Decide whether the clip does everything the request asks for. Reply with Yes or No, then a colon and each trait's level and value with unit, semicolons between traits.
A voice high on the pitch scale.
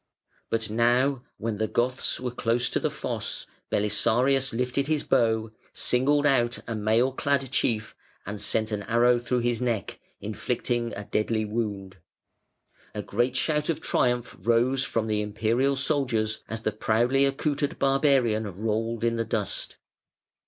No: low, 120 Hz